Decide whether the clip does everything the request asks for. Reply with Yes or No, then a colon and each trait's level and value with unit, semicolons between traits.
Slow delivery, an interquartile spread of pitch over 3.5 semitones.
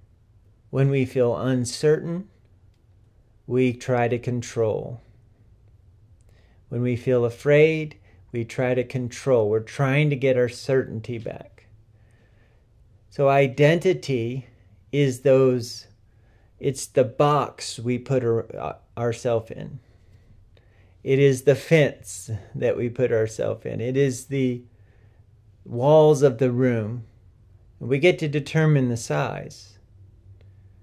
Yes: slow, 110 wpm; average, 4.2 semitones